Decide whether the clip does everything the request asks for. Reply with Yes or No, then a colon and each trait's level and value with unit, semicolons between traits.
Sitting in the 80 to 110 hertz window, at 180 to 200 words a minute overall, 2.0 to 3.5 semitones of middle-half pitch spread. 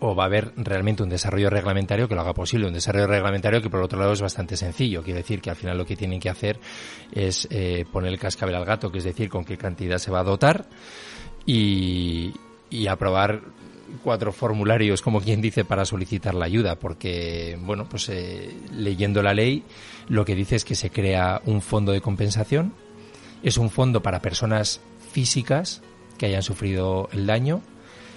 Yes: low, 100 Hz; fast, 190 wpm; average, 2.9 semitones